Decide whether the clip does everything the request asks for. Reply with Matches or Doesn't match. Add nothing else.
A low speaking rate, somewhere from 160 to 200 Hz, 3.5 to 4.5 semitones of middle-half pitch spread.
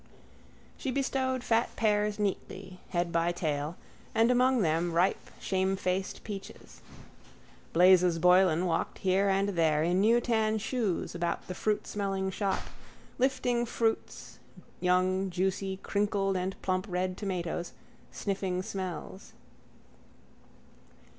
Doesn't match